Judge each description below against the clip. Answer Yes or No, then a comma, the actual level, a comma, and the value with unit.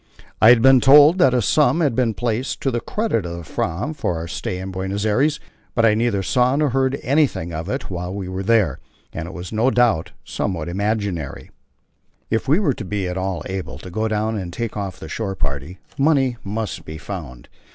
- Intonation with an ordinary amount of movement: No, wide, 5.7 semitones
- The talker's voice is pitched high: No, low, 105 Hz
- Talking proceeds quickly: Yes, fast, 215 wpm